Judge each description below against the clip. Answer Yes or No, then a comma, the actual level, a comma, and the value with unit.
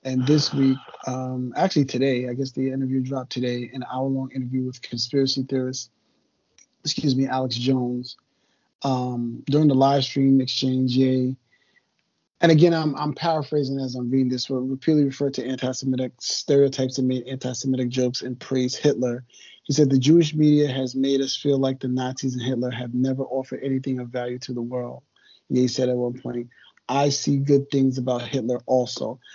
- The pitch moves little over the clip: Yes, narrow, 1.3 semitones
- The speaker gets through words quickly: No, average, 175 wpm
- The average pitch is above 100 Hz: Yes, low, 130 Hz